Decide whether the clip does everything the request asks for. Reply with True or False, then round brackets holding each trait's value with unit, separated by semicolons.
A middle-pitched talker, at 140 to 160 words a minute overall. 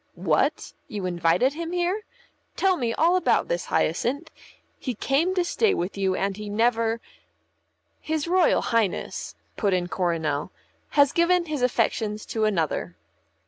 False (235 Hz; 145 wpm)